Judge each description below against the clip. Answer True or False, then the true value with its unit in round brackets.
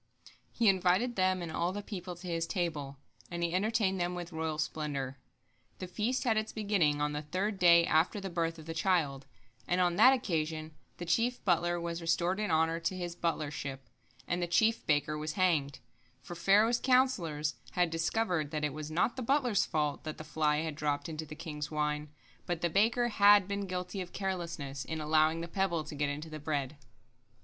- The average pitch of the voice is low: False (170 Hz)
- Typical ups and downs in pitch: True (3.7 semitones)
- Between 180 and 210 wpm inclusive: True (195 wpm)